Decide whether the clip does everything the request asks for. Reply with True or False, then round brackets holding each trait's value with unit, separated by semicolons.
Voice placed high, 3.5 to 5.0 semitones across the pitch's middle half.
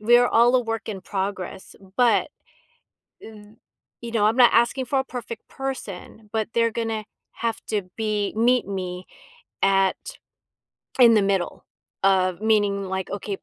False (215 Hz; 3.0 semitones)